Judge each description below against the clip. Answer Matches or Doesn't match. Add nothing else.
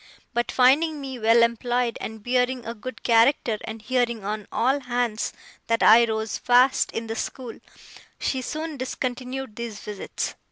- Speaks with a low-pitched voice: Doesn't match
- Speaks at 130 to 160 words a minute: Matches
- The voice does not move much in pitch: Matches